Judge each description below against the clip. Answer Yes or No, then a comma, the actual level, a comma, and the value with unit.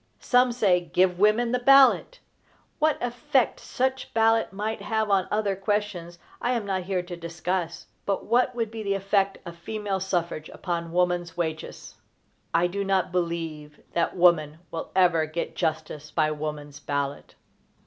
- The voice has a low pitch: No, medium, 185 Hz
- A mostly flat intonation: No, average, 4.3 semitones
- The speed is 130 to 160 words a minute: Yes, average, 155 wpm